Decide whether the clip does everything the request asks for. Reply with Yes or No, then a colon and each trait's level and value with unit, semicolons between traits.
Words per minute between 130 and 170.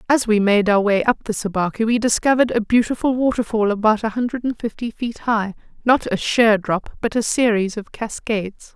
No: average, 190 wpm